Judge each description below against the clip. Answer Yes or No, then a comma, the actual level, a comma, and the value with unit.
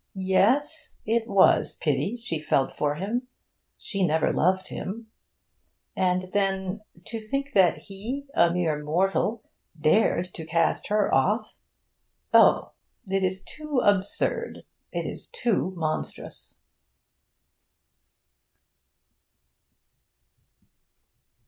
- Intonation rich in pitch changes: No, average, 4.2 semitones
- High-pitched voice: Yes, high, 195 Hz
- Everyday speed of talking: No, slow, 100 wpm